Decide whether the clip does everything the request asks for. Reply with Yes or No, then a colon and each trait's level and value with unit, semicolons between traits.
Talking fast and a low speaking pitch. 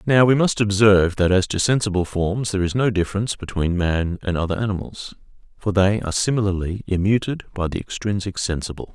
No: average, 180 wpm; low, 100 Hz